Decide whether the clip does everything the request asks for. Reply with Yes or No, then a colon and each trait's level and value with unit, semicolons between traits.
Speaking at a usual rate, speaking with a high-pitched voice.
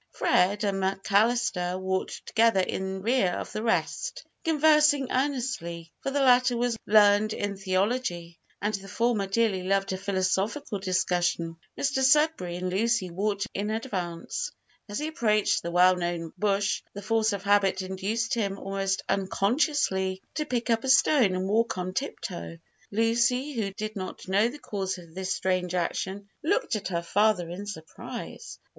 Yes: average, 160 wpm; high, 200 Hz